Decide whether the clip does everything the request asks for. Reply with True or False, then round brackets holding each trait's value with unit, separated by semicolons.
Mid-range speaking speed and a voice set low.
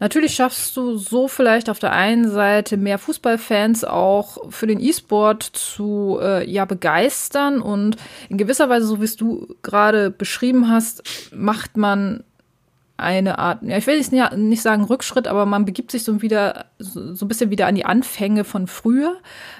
False (175 wpm; 215 Hz)